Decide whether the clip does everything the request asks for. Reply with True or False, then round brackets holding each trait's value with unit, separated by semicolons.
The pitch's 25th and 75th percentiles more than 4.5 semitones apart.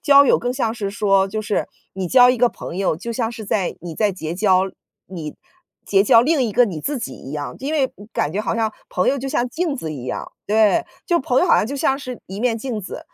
True (5.0 semitones)